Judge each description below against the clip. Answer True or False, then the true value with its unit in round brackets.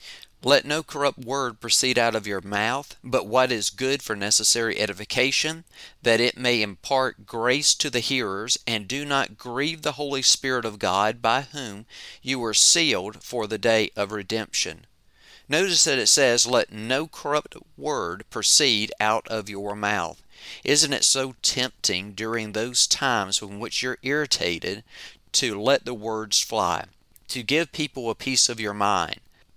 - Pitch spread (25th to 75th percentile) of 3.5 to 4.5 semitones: True (3.8 semitones)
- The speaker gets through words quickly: False (160 wpm)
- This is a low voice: True (115 Hz)